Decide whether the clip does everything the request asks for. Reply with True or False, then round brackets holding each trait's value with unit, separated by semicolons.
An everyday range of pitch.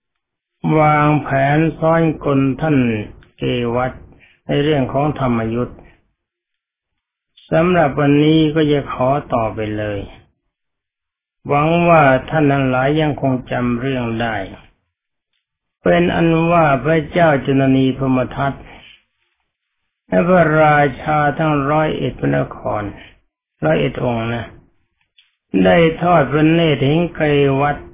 True (3.7 semitones)